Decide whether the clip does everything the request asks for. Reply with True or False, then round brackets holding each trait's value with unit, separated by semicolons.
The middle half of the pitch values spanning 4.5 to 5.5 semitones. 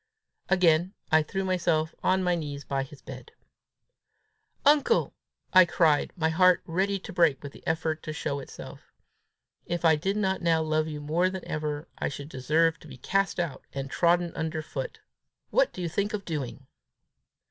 False (3.3 semitones)